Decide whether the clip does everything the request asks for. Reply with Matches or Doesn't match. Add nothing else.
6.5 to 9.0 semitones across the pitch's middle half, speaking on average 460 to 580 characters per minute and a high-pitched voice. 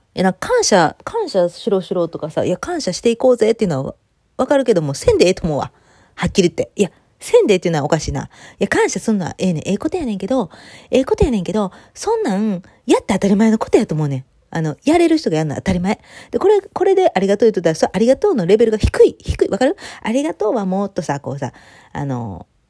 Matches